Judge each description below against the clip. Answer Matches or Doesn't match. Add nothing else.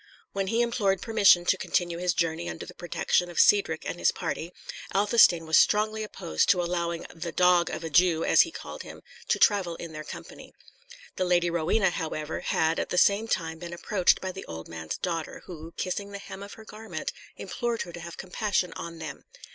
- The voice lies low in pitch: Doesn't match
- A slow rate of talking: Doesn't match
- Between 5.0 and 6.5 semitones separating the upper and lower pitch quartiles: Doesn't match